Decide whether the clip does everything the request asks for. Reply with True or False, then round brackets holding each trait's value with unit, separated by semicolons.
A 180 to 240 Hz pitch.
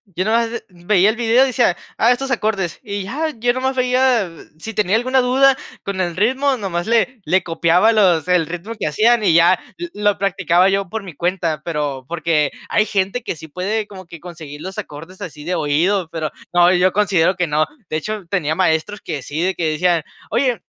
True (190 Hz)